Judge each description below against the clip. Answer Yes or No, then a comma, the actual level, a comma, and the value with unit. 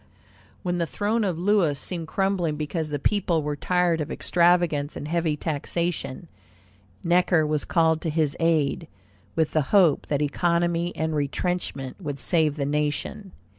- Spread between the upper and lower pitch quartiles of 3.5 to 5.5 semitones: No, average, 2.9 semitones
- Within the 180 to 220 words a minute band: No, average, 150 wpm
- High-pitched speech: No, medium, 165 Hz